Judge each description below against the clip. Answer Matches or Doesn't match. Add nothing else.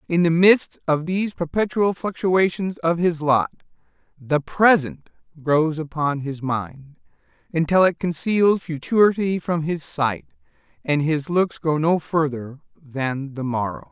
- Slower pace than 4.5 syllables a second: Matches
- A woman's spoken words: Doesn't match